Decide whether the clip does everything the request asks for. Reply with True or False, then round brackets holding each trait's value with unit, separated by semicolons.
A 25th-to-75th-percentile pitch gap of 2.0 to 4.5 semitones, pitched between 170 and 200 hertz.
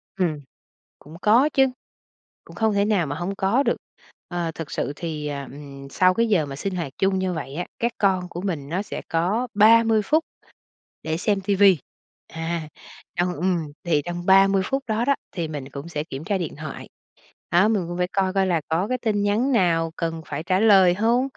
True (4.0 semitones; 185 Hz)